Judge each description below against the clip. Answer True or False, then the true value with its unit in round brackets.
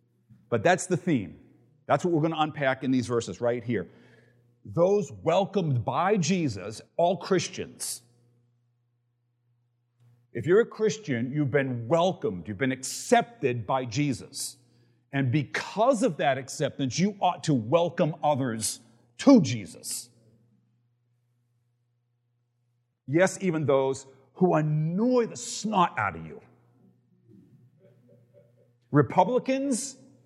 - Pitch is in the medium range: False (130 Hz)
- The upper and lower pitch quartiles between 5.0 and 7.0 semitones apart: True (5.3 semitones)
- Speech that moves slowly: True (110 wpm)